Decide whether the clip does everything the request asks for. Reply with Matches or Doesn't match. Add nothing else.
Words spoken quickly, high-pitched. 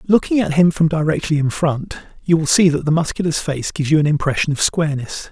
Doesn't match